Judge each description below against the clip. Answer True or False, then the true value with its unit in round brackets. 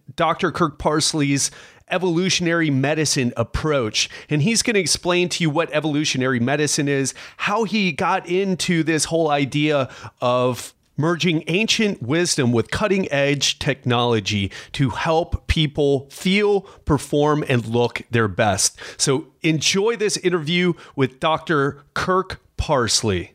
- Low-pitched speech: False (150 Hz)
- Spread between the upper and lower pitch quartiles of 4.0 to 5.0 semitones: True (4.6 semitones)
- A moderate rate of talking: False (125 wpm)